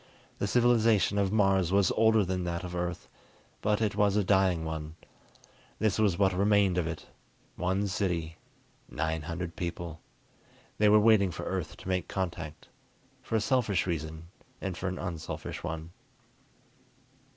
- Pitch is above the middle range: No, very low, 95 Hz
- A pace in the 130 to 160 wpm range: Yes, average, 150 wpm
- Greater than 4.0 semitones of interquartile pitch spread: No, average, 3.3 semitones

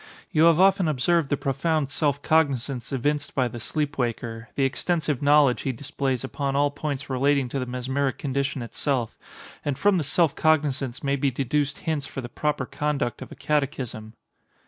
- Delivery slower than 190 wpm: Yes, average, 170 wpm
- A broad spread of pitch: No, narrow, 2.5 semitones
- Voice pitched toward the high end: No, medium, 140 Hz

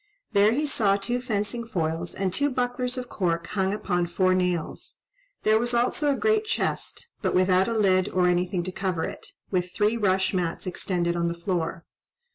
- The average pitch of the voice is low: No, high, 190 Hz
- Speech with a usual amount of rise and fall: Yes, average, 4.6 semitones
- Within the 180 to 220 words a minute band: Yes, average, 185 wpm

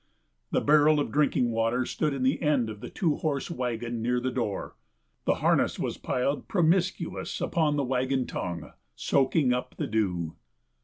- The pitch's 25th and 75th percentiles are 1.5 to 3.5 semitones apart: No, average, 4.2 semitones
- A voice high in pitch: No, low, 130 Hz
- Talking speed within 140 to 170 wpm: Yes, average, 165 wpm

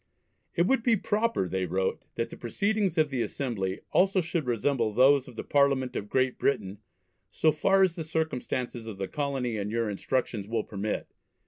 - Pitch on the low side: Yes, low, 130 Hz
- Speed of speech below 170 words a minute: No, average, 185 wpm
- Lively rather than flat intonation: Yes, wide, 6.8 semitones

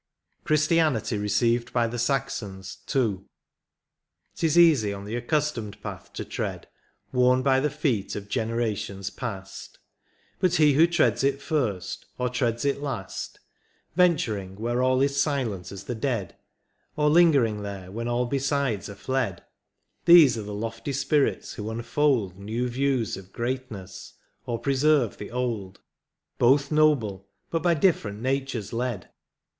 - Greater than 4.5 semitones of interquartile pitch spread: Yes, average, 5.1 semitones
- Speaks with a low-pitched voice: Yes, low, 120 Hz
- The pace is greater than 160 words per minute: No, average, 150 wpm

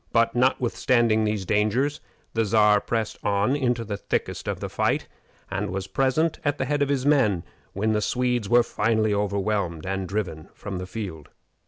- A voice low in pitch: Yes, low, 110 Hz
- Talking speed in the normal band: Yes, average, 175 wpm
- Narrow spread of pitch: No, average, 3.8 semitones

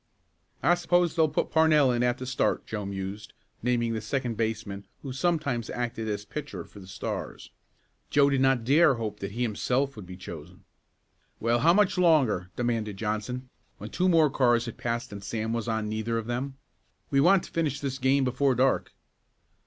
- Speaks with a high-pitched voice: No, low, 120 Hz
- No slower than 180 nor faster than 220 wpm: Yes, average, 185 wpm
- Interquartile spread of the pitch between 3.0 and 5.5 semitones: Yes, average, 4.2 semitones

